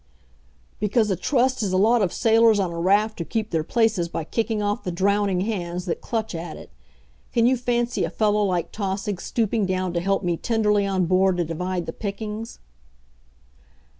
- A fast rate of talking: No, average, 190 wpm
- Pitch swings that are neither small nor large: Yes, average, 3.6 semitones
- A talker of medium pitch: No, high, 200 Hz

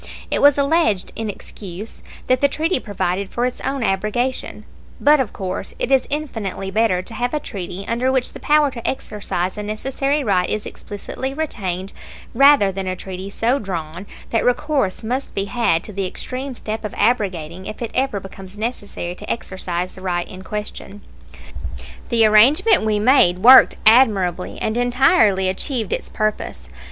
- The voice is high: Yes, high, 215 Hz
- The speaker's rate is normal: Yes, average, 165 wpm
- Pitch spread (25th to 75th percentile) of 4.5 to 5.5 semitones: Yes, average, 5.1 semitones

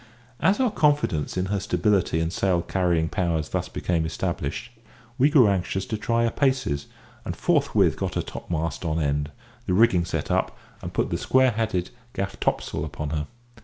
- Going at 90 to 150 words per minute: No, average, 175 wpm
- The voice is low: Yes, very low, 90 Hz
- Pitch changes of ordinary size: No, wide, 6.0 semitones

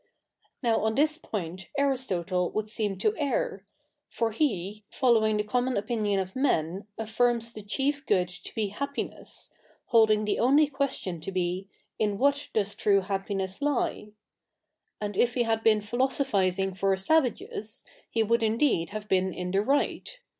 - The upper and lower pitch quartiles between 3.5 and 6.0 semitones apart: Yes, average, 4.4 semitones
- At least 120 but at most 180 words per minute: Yes, average, 160 wpm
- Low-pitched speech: No, high, 215 Hz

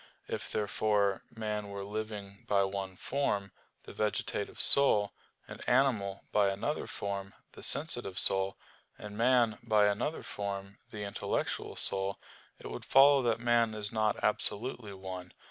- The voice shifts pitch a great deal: No, average, 2.7 semitones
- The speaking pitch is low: Yes, low, 105 Hz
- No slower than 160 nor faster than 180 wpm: No, average, 140 wpm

